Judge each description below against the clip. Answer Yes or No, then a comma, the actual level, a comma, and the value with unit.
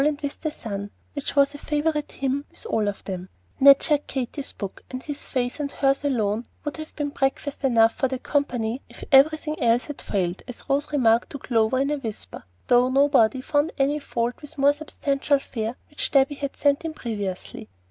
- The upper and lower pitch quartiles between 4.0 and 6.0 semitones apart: No, average, 3.6 semitones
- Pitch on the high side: Yes, very high, 275 Hz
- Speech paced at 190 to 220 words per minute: Yes, average, 200 wpm